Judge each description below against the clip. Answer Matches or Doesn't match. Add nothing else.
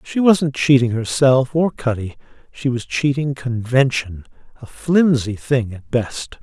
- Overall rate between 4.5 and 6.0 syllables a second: Doesn't match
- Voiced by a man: Matches